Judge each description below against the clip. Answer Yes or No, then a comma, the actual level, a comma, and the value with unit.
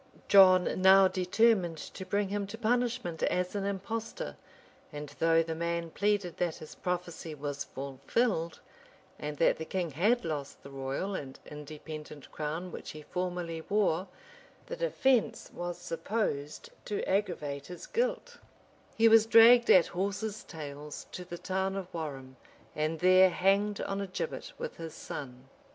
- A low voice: No, medium, 180 Hz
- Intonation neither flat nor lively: Yes, average, 4.6 semitones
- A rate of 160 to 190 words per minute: No, average, 150 wpm